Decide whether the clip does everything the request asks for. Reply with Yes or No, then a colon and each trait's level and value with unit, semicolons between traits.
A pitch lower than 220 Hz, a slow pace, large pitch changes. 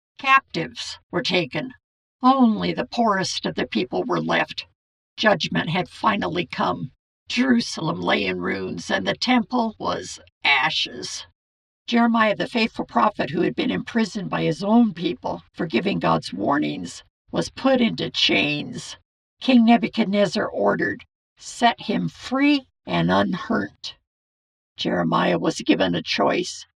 No: high, 225 Hz; slow, 130 wpm; wide, 7.1 semitones